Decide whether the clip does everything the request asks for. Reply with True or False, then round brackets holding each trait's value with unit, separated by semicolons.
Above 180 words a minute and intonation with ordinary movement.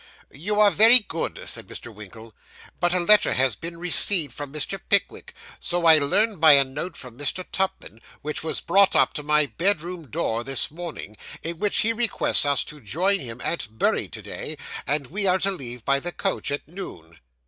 False (195 wpm; 5.7 semitones)